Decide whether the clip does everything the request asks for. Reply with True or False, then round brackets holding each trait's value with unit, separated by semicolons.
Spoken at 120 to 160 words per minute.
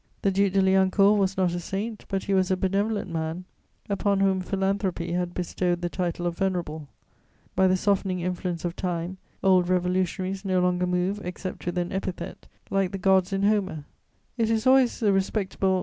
False (185 wpm)